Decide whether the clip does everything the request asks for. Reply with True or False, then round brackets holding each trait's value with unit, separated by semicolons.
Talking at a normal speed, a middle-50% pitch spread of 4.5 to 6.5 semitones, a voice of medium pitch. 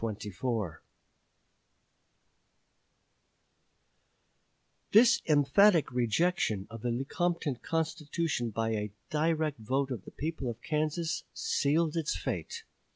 False (90 wpm; 5.5 semitones; 145 Hz)